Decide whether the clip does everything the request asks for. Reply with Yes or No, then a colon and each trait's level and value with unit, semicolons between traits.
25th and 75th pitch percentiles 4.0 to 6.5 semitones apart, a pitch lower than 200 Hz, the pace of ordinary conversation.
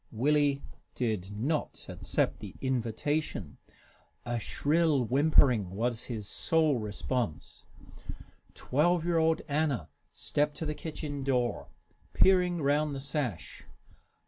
No: average, 4.5 semitones; medium, 140 Hz; slow, 110 wpm